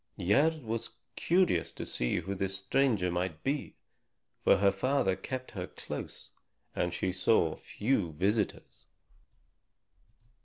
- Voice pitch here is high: No, low, 100 Hz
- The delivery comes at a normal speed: No, slow, 120 wpm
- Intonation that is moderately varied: No, wide, 6.0 semitones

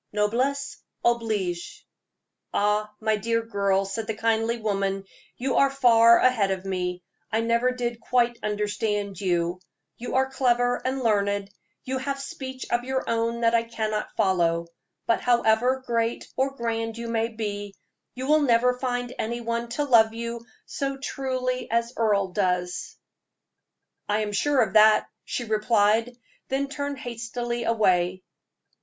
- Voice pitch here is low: No, high, 230 Hz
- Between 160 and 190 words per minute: No, average, 145 wpm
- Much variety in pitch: No, average, 3.0 semitones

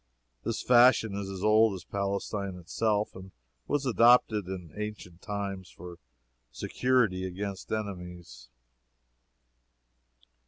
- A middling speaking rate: No, slow, 105 wpm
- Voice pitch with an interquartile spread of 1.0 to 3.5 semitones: Yes, average, 2.9 semitones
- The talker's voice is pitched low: Yes, low, 100 Hz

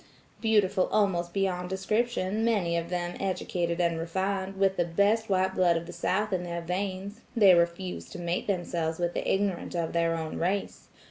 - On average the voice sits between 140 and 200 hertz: Yes, medium, 185 Hz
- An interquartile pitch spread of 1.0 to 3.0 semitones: Yes, narrow, 2.4 semitones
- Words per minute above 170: Yes, average, 180 wpm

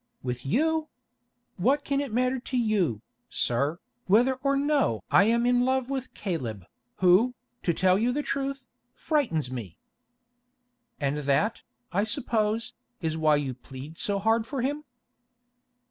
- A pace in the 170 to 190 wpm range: No, average, 145 wpm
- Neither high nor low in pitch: No, high, 220 Hz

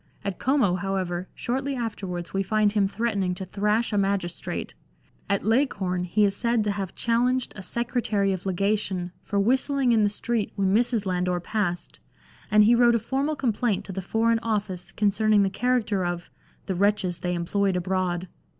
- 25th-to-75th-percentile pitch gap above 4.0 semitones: No, average, 3.6 semitones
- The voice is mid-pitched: No, high, 205 Hz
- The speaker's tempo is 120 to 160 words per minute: No, average, 175 wpm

